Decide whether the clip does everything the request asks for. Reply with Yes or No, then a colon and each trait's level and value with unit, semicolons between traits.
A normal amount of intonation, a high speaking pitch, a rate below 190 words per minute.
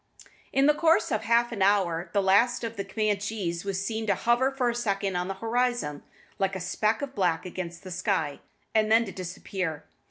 No: average, 3.8 semitones; high, 200 Hz; average, 200 wpm